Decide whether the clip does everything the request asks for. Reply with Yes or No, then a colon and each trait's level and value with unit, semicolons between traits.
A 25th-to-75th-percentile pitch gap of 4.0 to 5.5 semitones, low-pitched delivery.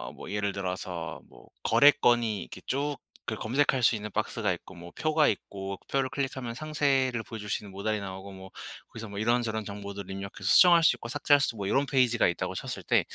Yes: average, 5.2 semitones; low, 110 Hz